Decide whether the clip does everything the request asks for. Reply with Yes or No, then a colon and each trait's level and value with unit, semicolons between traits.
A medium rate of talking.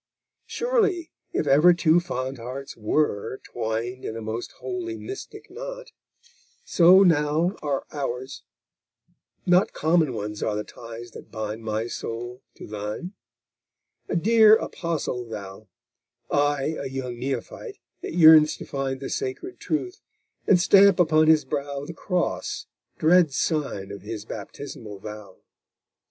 No: slow, 130 wpm